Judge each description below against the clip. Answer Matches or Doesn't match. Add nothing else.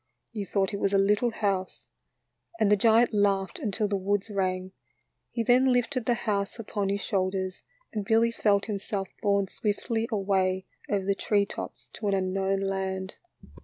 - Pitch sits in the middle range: Doesn't match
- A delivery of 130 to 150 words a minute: Doesn't match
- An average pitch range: Doesn't match